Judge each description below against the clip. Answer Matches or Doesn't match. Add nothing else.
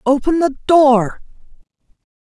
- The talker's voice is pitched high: Matches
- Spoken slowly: Matches